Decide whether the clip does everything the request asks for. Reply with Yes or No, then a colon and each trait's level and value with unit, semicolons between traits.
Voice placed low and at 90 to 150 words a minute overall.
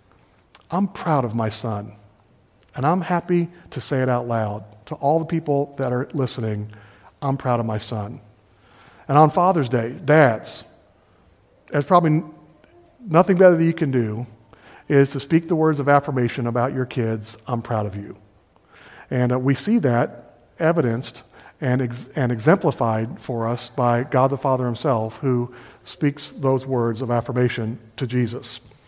No: low, 130 Hz; average, 160 wpm